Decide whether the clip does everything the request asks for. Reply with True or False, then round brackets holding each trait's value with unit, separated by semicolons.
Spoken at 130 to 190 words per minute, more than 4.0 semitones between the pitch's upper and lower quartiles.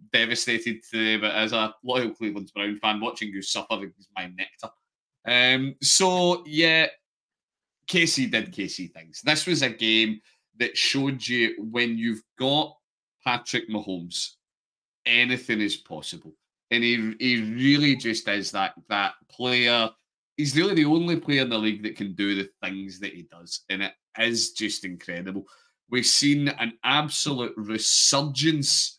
True (150 wpm; 4.4 semitones)